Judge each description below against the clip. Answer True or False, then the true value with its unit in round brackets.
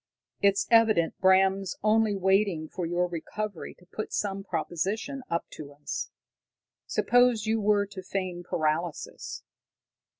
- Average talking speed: False (125 wpm)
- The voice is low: False (195 Hz)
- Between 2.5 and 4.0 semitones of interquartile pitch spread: True (3.5 semitones)